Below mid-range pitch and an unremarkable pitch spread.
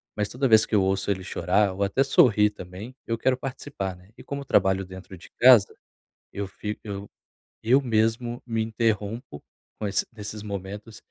Yes: low, 105 Hz; average, 3.1 semitones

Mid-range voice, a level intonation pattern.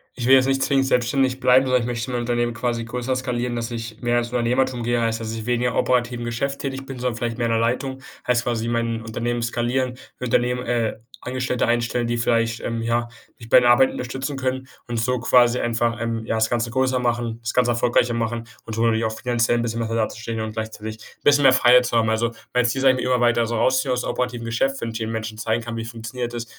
No: low, 120 Hz; narrow, 1.5 semitones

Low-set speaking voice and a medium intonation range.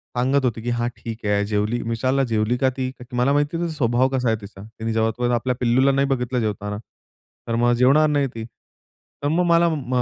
Yes: low, 125 Hz; average, 3.2 semitones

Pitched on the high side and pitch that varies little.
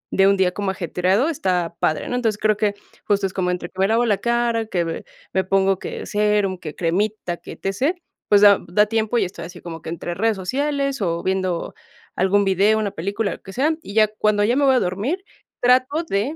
No: high, 200 Hz; average, 3.4 semitones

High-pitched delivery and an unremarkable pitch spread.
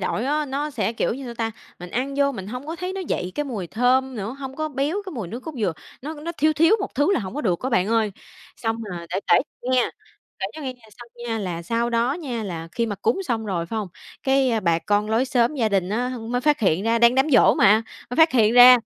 Yes: high, 240 Hz; average, 4.5 semitones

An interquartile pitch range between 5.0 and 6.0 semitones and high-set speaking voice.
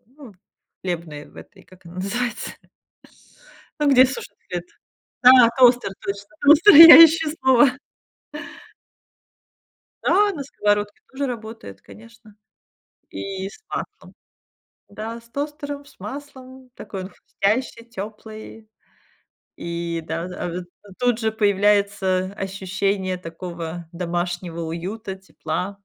Yes: wide, 5.5 semitones; high, 205 Hz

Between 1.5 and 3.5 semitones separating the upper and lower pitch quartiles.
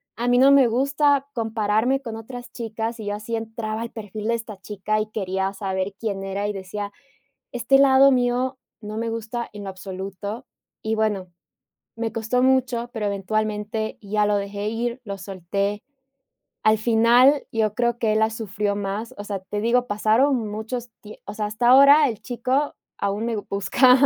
Yes: average, 2.9 semitones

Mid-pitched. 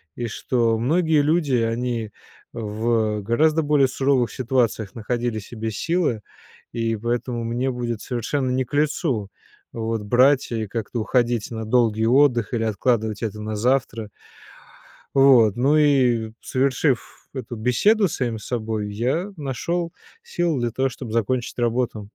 No: low, 120 Hz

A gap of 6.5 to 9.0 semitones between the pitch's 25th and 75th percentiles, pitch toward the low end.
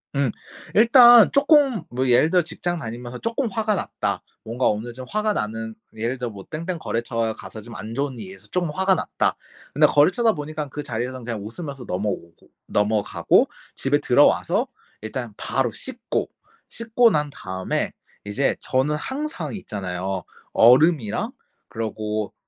Yes: wide, 8.5 semitones; low, 130 Hz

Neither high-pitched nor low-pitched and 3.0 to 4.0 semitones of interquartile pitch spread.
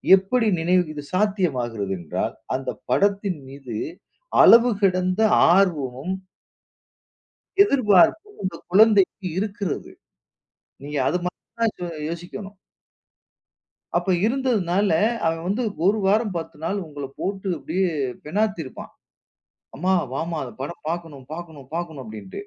No: medium, 180 Hz; average, 5.1 semitones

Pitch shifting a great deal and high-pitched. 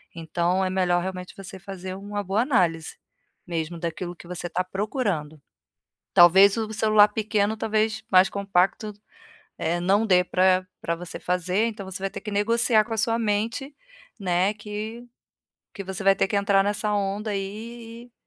No: average, 2.9 semitones; high, 195 Hz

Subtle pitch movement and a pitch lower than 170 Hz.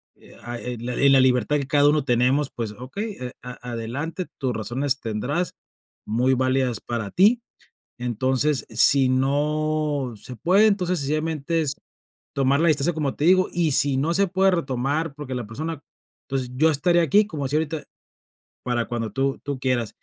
No: average, 3.9 semitones; medium, 140 Hz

